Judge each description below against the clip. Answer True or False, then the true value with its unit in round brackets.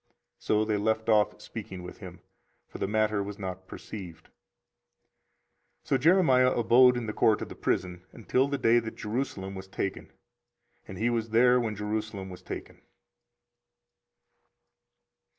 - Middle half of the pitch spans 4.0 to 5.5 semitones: False (3.4 semitones)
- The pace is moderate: True (150 wpm)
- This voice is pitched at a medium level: False (110 Hz)